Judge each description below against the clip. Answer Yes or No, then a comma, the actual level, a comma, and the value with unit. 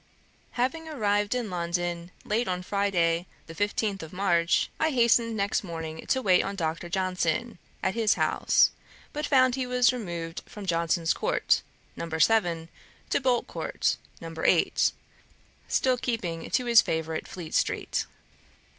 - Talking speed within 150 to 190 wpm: No, average, 140 wpm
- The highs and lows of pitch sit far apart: Yes, wide, 5.8 semitones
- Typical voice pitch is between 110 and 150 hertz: No, high, 195 Hz